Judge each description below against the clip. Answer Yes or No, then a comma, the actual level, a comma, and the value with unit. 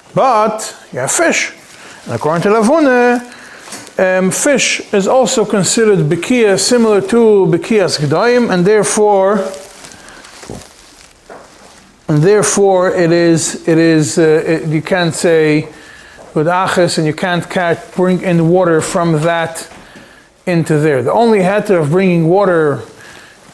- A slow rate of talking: Yes, slow, 125 wpm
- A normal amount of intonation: Yes, average, 4.1 semitones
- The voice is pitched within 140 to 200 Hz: Yes, medium, 185 Hz